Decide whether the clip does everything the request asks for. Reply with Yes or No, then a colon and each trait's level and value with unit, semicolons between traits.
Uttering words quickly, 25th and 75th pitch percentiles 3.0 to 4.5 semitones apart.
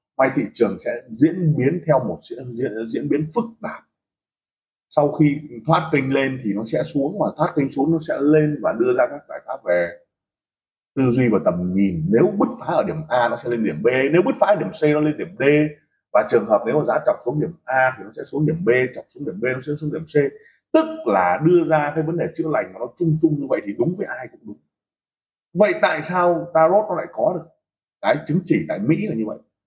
Yes: fast, 255 wpm; average, 3.4 semitones